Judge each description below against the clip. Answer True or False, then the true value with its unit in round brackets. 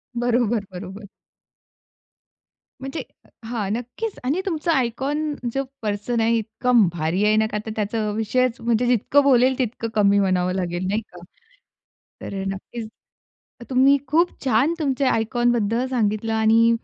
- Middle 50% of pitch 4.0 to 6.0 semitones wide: False (3.4 semitones)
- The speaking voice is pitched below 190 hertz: False (230 Hz)